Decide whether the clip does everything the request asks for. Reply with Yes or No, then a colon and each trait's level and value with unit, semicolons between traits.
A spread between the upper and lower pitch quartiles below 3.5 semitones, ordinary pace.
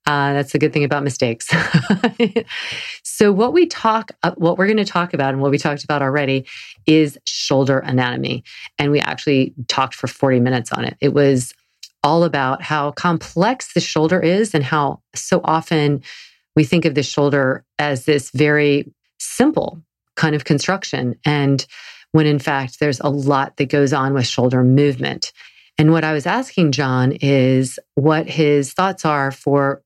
Yes: average, 2.9 semitones; average, 170 wpm